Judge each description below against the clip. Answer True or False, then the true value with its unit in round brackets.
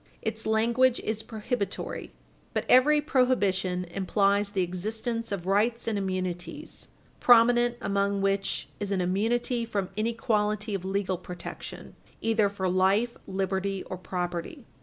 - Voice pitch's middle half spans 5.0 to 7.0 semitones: False (3.3 semitones)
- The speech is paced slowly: True (125 wpm)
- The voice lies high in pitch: True (205 Hz)